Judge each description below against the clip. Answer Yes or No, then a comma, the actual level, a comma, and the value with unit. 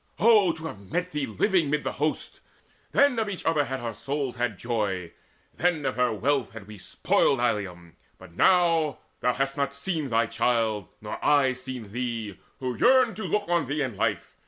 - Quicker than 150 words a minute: Yes, average, 190 wpm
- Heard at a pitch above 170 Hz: No, low, 135 Hz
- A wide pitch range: Yes, wide, 6.2 semitones